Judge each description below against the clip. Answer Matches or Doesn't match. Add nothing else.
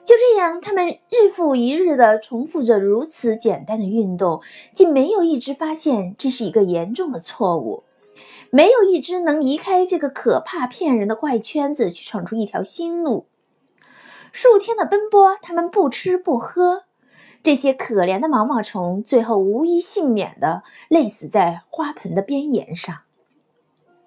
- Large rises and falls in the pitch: Matches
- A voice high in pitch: Matches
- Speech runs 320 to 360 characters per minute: Doesn't match